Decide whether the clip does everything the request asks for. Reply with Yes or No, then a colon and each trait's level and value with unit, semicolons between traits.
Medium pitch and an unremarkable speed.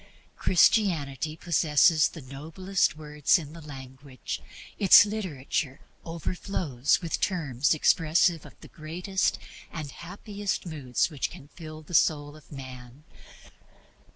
No: medium, 155 Hz; slow, 115 wpm